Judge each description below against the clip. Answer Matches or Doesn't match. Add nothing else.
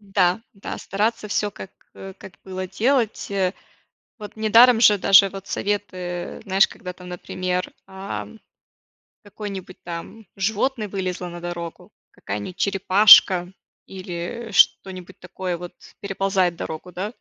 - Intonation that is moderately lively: Doesn't match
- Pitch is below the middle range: Doesn't match